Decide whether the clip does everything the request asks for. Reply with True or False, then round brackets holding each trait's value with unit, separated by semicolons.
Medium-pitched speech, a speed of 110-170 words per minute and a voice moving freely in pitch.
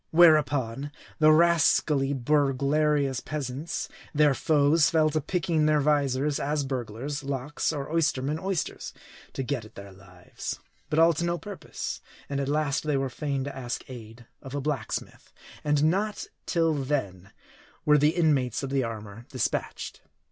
False (145 Hz; 150 wpm; 2.7 semitones)